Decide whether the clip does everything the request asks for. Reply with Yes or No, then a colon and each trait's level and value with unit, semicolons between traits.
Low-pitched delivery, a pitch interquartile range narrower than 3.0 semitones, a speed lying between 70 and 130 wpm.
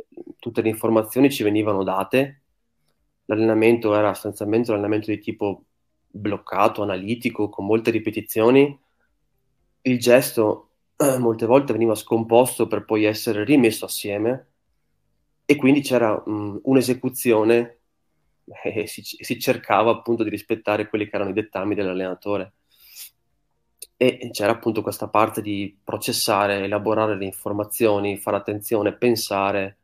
Yes: low, 110 Hz; narrow, 2.4 semitones; average, 120 wpm